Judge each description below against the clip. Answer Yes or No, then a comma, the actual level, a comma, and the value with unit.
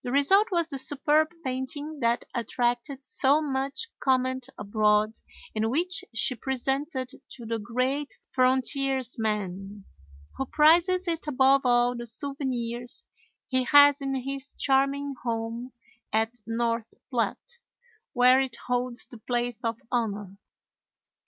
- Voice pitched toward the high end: Yes, very high, 255 Hz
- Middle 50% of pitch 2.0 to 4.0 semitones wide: Yes, average, 2.9 semitones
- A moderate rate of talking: No, slow, 120 wpm